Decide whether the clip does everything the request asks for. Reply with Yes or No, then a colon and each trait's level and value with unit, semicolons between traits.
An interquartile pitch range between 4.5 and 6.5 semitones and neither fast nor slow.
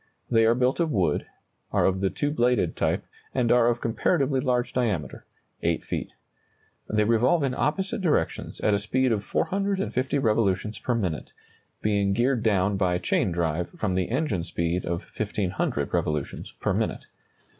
Yes: wide, 5.4 semitones; average, 160 wpm